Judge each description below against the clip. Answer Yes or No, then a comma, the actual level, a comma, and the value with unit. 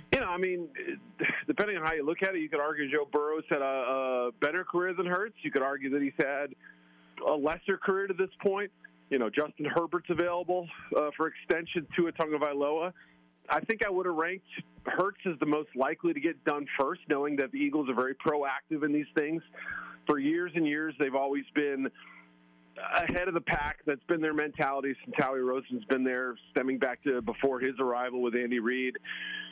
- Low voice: No, medium, 150 Hz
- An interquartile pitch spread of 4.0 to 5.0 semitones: Yes, average, 4.5 semitones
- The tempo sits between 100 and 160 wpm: No, fast, 205 wpm